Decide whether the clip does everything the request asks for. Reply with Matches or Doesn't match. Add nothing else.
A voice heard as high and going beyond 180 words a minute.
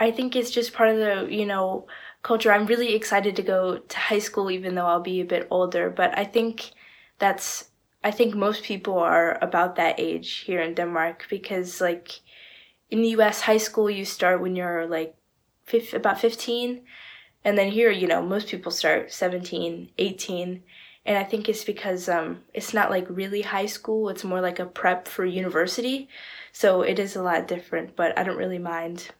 Matches